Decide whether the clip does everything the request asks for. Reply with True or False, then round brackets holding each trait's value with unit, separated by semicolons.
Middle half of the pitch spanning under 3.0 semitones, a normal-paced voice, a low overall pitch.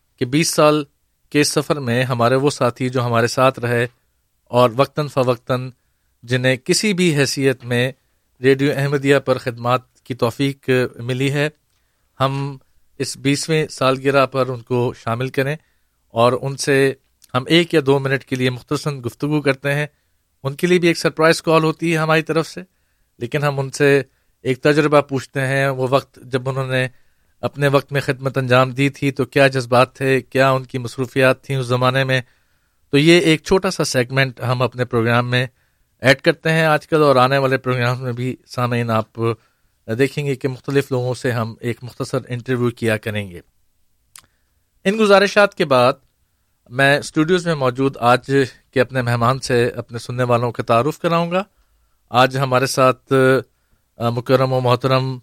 True (2.5 semitones; 170 wpm; 130 Hz)